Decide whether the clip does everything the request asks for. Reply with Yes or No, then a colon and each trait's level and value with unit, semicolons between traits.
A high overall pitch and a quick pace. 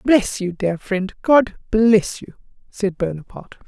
No: high, 200 Hz; average, 145 wpm